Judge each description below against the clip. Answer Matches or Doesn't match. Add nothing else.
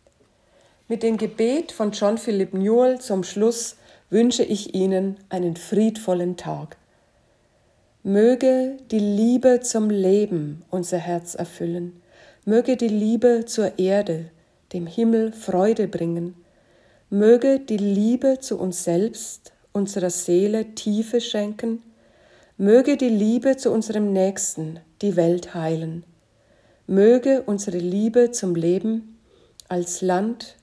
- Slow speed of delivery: Matches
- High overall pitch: Matches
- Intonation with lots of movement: Doesn't match